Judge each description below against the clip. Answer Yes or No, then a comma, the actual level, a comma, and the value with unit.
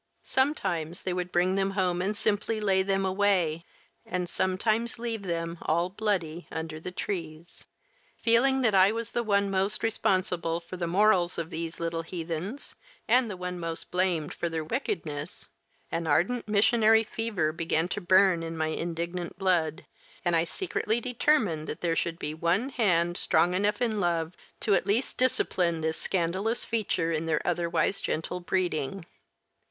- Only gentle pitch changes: No, average, 3.8 semitones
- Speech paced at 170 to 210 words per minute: No, average, 160 wpm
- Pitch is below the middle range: No, medium, 180 Hz